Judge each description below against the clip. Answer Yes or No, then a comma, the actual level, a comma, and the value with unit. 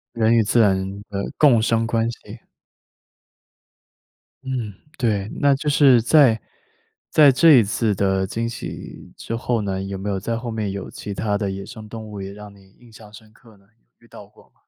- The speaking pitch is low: Yes, low, 110 Hz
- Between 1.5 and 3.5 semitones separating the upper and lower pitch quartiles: Yes, average, 2.8 semitones